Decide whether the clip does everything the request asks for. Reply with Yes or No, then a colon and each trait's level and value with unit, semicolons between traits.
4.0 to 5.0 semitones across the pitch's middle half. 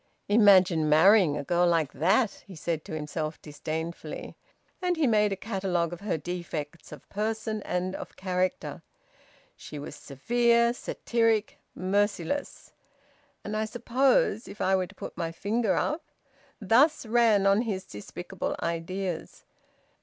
Yes: average, 4.7 semitones